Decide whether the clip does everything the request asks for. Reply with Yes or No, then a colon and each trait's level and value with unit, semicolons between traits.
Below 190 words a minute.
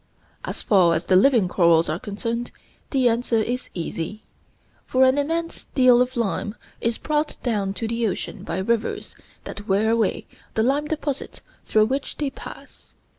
Yes: average, 165 wpm